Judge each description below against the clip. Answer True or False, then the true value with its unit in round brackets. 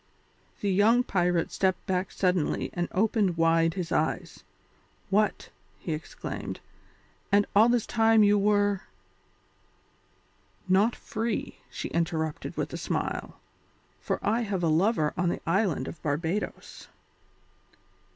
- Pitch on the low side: False (190 Hz)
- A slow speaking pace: True (125 wpm)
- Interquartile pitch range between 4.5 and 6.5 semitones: False (4.0 semitones)